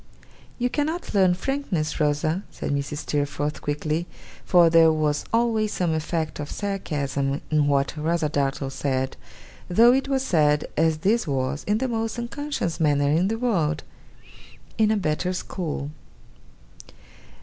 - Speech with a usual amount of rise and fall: No, wide, 6.4 semitones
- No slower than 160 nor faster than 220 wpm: No, average, 140 wpm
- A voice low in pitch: No, medium, 160 Hz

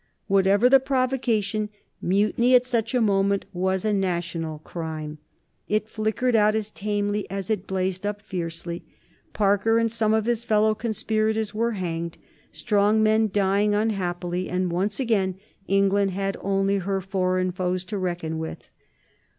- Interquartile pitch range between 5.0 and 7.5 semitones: No, average, 2.9 semitones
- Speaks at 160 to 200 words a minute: No, average, 145 wpm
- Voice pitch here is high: Yes, high, 200 Hz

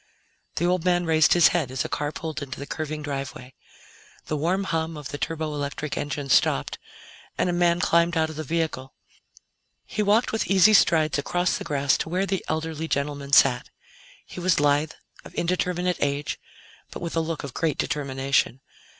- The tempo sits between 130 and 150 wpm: No, average, 180 wpm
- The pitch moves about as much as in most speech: Yes, average, 3.3 semitones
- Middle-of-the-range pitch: Yes, medium, 160 Hz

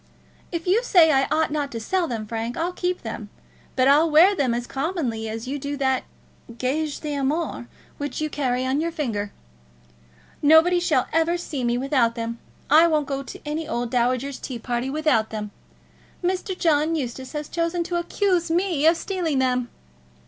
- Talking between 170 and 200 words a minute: Yes, average, 180 wpm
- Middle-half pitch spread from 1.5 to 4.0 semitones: No, average, 4.8 semitones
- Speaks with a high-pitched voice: Yes, very high, 290 Hz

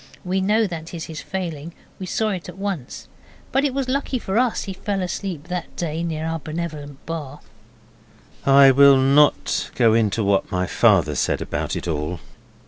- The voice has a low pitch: No, medium, 165 Hz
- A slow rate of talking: No, average, 180 wpm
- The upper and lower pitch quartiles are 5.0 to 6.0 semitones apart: Yes, wide, 5.6 semitones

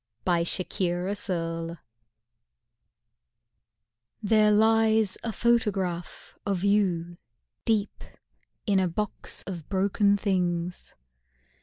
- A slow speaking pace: Yes, slow, 75 wpm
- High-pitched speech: Yes, high, 195 Hz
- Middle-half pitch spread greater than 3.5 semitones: No, average, 3.2 semitones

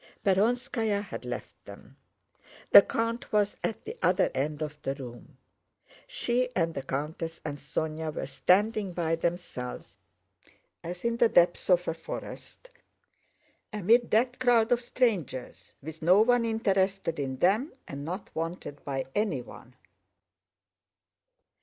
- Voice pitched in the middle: Yes, medium, 180 Hz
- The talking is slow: Yes, slow, 130 wpm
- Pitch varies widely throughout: Yes, wide, 6.5 semitones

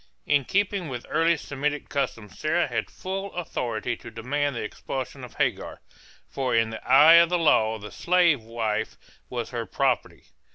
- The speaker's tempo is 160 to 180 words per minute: Yes, average, 165 wpm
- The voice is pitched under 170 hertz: Yes, low, 135 Hz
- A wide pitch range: Yes, wide, 6.5 semitones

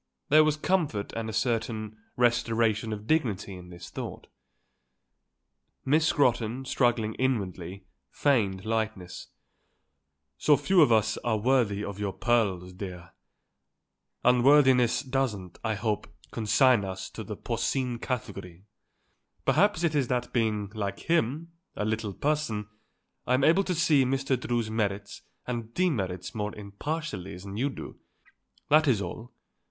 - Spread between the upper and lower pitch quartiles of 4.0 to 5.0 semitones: Yes, average, 4.6 semitones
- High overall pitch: No, low, 115 Hz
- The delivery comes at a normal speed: No, slow, 130 wpm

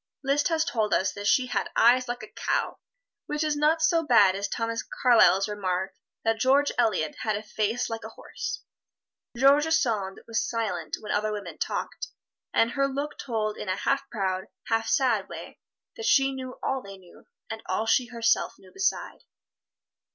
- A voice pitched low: No, high, 230 Hz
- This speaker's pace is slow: No, average, 180 wpm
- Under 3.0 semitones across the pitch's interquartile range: No, average, 4.8 semitones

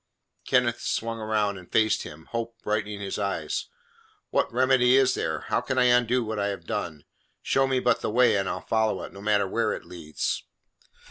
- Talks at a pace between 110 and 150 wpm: No, average, 195 wpm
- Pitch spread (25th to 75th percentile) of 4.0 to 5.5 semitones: No, average, 3.5 semitones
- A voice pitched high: No, low, 110 Hz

